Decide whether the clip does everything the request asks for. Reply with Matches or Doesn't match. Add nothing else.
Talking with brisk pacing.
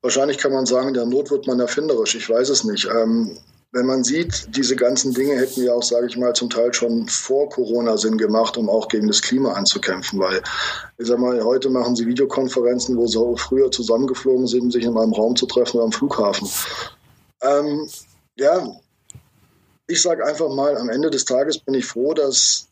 Matches